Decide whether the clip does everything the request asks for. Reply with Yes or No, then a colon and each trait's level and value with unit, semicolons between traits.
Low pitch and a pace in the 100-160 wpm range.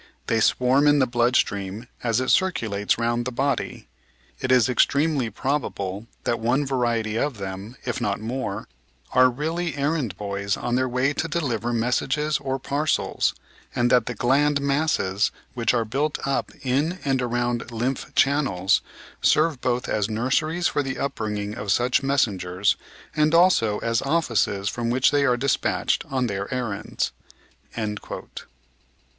Yes: low, 125 Hz; average, 150 wpm